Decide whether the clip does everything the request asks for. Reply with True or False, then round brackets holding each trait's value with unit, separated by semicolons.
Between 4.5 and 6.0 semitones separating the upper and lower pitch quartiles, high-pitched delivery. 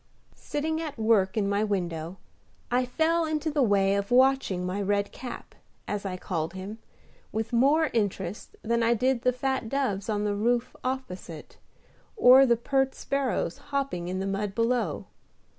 True (5.2 semitones; 225 Hz)